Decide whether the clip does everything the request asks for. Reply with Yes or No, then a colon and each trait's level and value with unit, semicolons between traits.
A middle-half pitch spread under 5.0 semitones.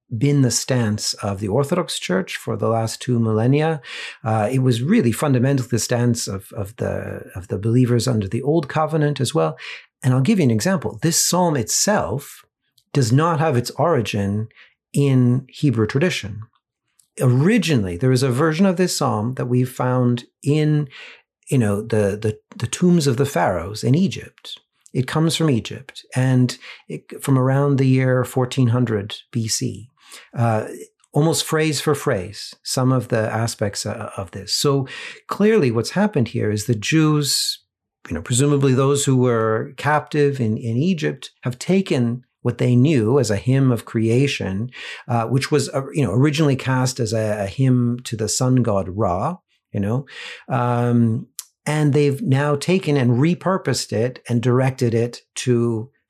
Yes: average, 3.9 semitones